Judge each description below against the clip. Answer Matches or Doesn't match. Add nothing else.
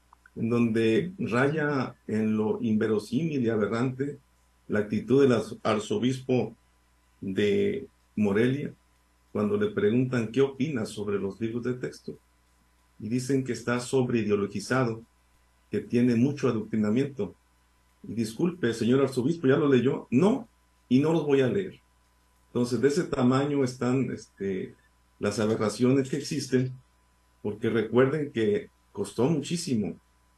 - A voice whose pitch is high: Doesn't match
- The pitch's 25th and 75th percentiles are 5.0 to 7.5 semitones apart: Matches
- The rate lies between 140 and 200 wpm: Doesn't match